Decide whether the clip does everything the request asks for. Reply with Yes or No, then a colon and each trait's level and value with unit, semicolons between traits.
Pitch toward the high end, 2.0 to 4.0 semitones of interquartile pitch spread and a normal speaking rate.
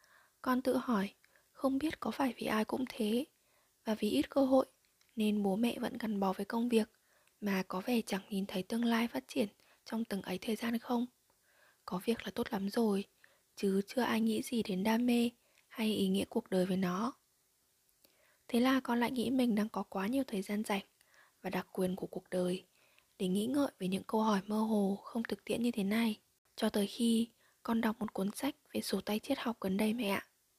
Yes: high, 220 Hz; average, 3.2 semitones; average, 220 wpm